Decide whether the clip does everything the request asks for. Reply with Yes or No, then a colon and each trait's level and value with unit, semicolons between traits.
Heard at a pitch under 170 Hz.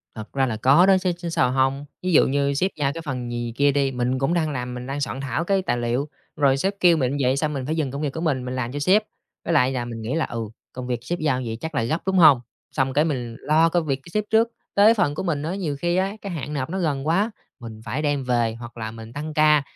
Yes: medium, 140 Hz